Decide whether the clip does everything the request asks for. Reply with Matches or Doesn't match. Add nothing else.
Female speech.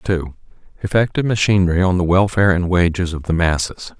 Doesn't match